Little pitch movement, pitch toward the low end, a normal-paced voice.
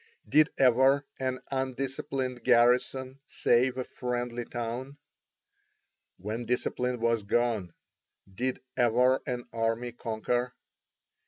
No: narrow, 1.7 semitones; low, 125 Hz; slow, 95 wpm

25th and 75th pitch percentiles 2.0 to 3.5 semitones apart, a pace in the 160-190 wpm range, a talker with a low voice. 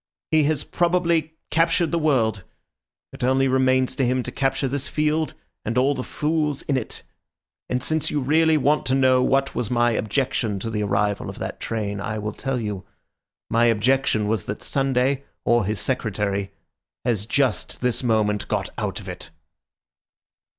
No: average, 4.4 semitones; average, 170 wpm; low, 130 Hz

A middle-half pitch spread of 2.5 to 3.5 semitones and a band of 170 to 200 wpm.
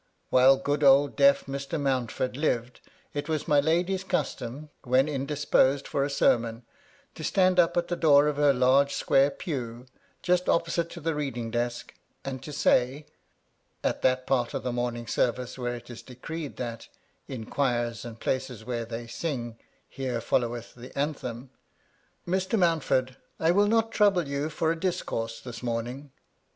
No: average, 4.0 semitones; average, 180 wpm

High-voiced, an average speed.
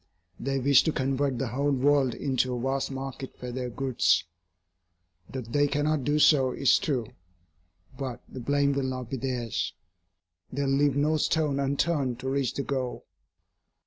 No: low, 135 Hz; average, 165 wpm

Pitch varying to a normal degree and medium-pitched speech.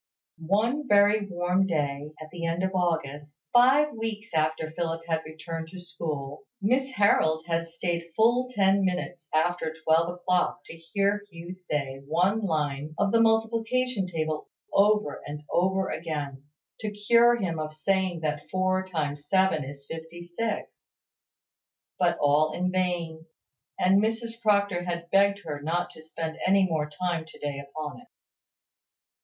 Yes: average, 4.1 semitones; medium, 175 Hz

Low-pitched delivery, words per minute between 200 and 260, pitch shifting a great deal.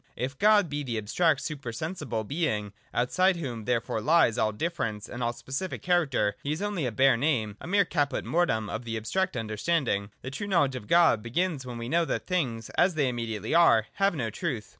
Yes: low, 130 Hz; fast, 205 wpm; wide, 7.0 semitones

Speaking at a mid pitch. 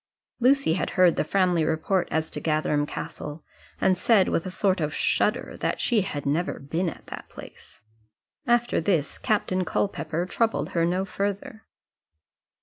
Yes: medium, 180 Hz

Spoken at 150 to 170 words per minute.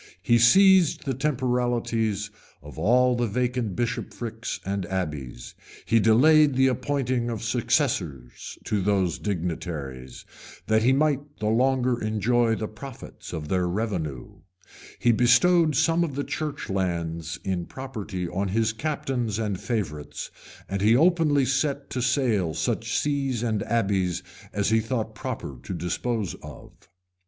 No: slow, 135 wpm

